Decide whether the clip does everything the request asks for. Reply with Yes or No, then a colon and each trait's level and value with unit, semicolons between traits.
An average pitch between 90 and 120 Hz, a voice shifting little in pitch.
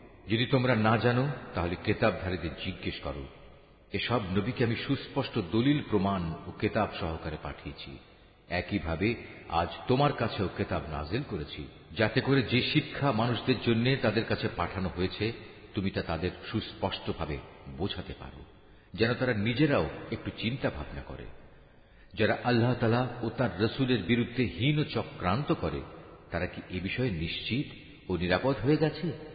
No: low, 105 Hz; wide, 5.4 semitones